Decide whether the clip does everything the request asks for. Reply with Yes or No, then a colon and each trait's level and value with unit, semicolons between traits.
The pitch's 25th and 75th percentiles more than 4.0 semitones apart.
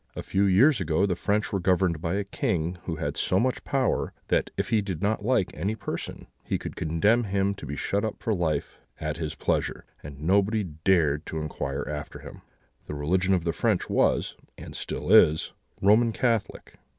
Yes: average, 4.5 semitones